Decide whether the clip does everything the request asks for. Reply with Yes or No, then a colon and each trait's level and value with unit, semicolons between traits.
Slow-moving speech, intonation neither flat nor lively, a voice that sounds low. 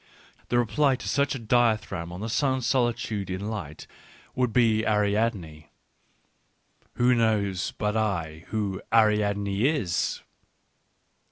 Yes: slow, 115 wpm; average, 3.6 semitones; low, 110 Hz